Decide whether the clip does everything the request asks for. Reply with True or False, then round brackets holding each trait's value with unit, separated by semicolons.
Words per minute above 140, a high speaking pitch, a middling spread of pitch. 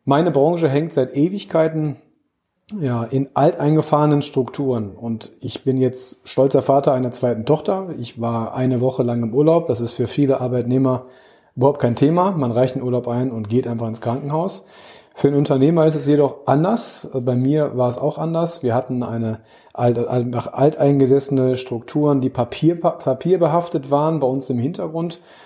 False (160 wpm; 135 Hz; 3.3 semitones)